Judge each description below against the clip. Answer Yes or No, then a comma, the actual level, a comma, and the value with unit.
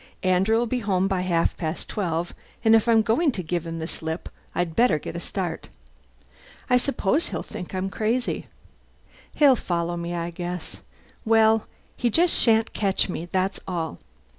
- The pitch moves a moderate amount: Yes, average, 4.6 semitones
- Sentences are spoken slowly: No, average, 165 wpm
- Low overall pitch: No, high, 190 Hz